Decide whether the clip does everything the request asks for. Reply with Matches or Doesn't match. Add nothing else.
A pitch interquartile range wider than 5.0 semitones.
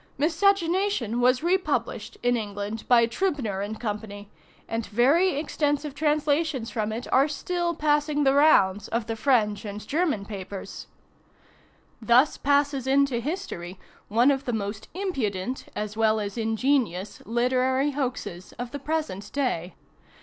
Matches